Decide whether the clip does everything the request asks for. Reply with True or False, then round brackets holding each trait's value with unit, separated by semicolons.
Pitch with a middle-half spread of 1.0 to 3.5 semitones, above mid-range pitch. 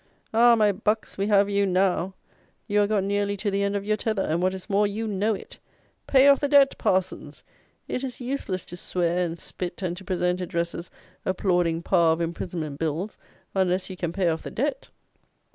True (2.9 semitones; 195 Hz)